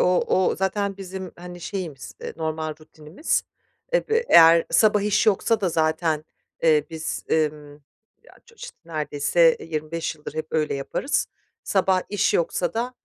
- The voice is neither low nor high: Yes, medium, 170 Hz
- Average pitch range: Yes, average, 3.9 semitones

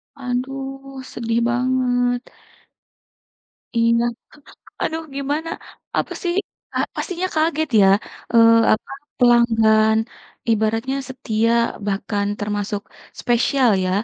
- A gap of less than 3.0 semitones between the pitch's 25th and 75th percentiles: No, average, 3.6 semitones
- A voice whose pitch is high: Yes, high, 245 Hz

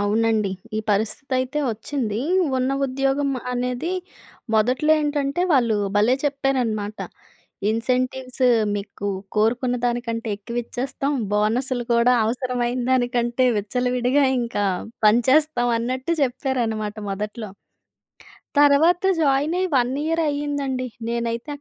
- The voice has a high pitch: Yes, very high, 250 Hz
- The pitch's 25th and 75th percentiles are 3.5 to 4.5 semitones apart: No, average, 3.0 semitones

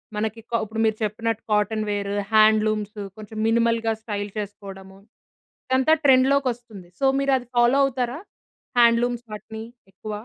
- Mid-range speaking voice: No, high, 220 Hz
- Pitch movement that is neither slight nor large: No, narrow, 2.3 semitones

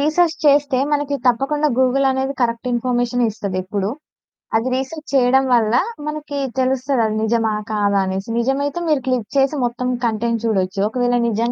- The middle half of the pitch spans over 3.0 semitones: Yes, average, 3.4 semitones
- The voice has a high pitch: Yes, very high, 250 Hz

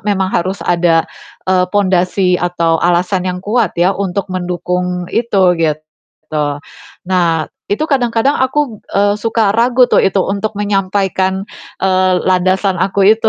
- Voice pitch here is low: No, high, 190 Hz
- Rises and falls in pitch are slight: Yes, narrow, 2.3 semitones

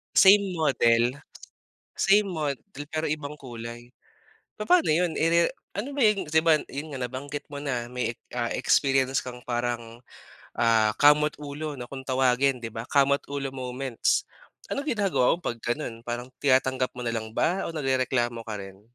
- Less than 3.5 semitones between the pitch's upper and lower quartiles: No, average, 4.2 semitones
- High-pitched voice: No, low, 135 Hz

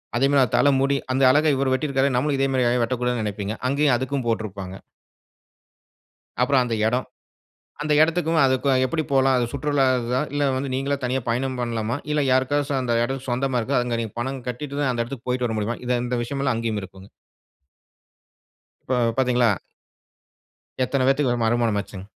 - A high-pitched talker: No, low, 130 Hz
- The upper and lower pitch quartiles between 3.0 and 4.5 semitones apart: No, narrow, 2.5 semitones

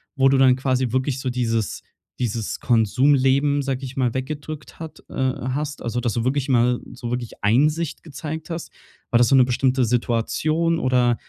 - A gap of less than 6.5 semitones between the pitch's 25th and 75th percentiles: Yes, average, 2.7 semitones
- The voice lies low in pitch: Yes, low, 130 Hz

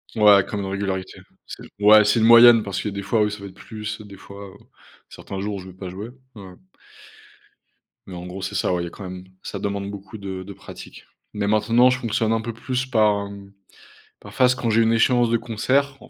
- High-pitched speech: No, low, 105 Hz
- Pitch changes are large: No, average, 2.7 semitones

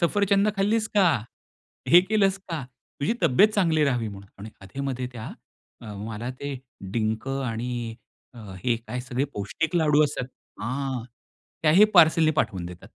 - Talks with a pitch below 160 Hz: Yes, low, 135 Hz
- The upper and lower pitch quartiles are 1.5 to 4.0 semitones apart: No, wide, 6.7 semitones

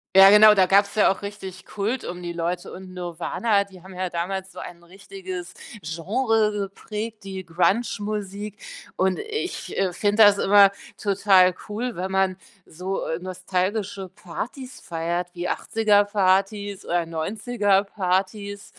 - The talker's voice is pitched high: Yes, high, 195 Hz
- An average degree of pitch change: No, narrow, 2.2 semitones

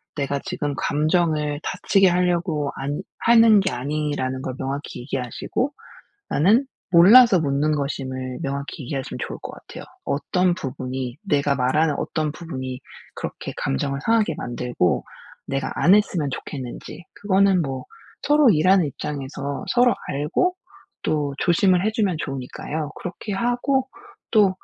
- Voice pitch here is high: No, medium, 150 Hz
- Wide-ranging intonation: Yes, wide, 5.7 semitones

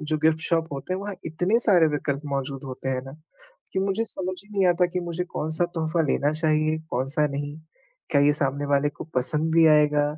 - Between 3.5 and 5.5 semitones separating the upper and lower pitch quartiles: No, average, 3.0 semitones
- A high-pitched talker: No, medium, 155 Hz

